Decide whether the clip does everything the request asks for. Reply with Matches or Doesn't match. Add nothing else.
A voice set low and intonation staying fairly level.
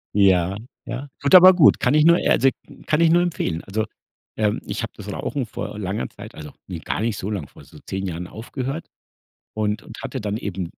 Doesn't match